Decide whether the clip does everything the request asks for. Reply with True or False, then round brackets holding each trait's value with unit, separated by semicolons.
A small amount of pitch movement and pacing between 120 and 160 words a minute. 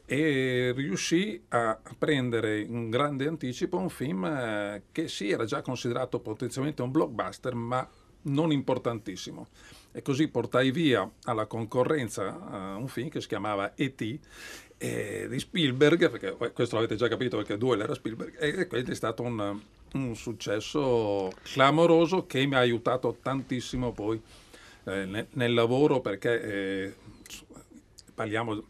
False (4.7 semitones; 145 wpm)